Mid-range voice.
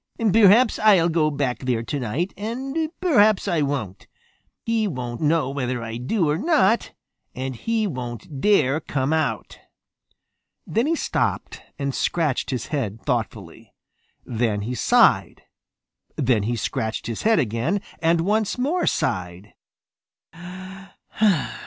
Yes: medium, 145 Hz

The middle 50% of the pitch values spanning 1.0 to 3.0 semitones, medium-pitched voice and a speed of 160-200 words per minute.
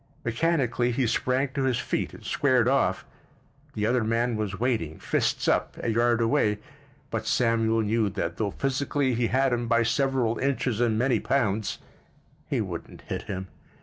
No: average, 2.7 semitones; low, 120 Hz; average, 165 wpm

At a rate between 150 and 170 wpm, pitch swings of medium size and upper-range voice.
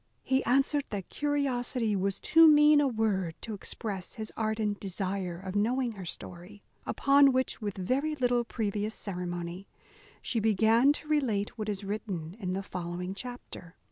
Yes: average, 155 wpm; average, 4.9 semitones; high, 215 Hz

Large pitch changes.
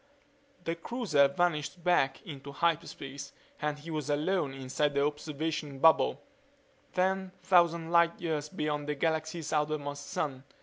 No: average, 2.8 semitones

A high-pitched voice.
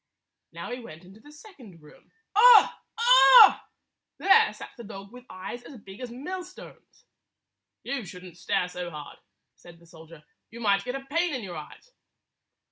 Yes: high, 225 Hz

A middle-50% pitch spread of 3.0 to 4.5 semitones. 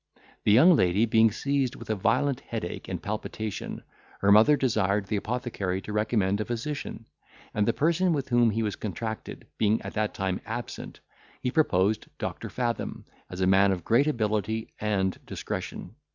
Yes: average, 3.4 semitones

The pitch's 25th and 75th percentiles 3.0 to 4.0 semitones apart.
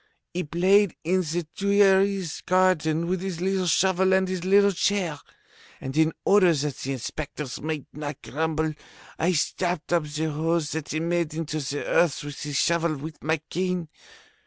Yes: average, 3.3 semitones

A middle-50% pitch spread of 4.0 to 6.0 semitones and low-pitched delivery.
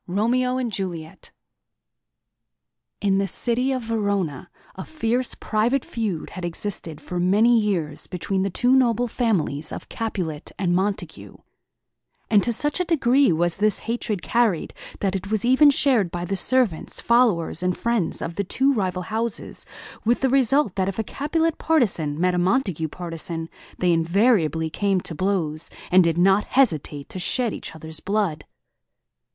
No: wide, 5.5 semitones; high, 200 Hz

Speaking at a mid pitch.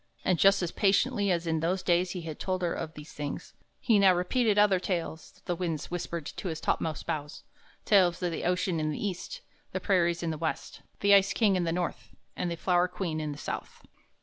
Yes: medium, 175 Hz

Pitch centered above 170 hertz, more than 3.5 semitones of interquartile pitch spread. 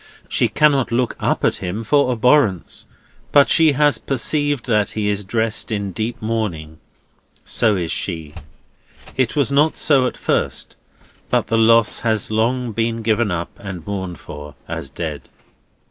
No: low, 110 Hz; average, 4.6 semitones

